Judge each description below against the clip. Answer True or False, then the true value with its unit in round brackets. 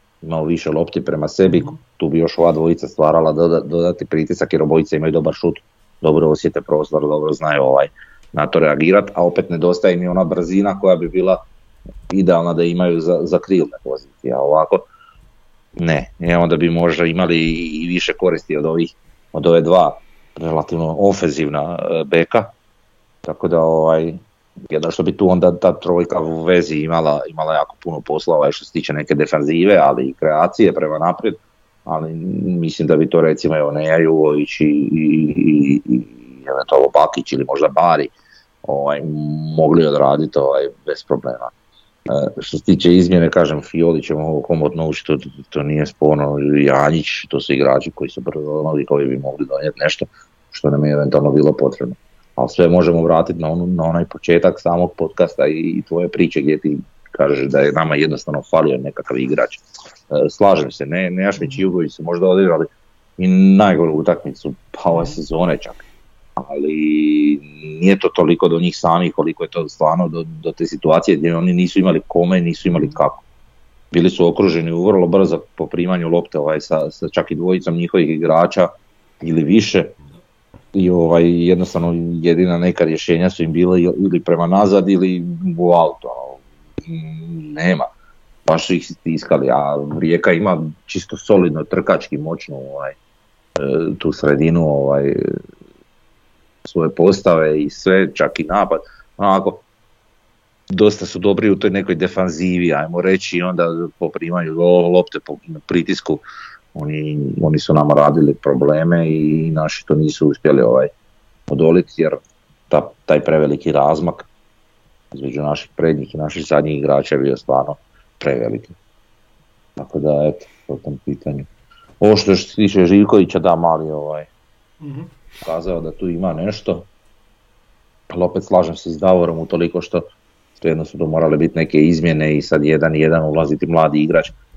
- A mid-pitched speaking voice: False (85 Hz)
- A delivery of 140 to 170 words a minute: True (160 wpm)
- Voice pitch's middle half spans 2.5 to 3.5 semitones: True (2.8 semitones)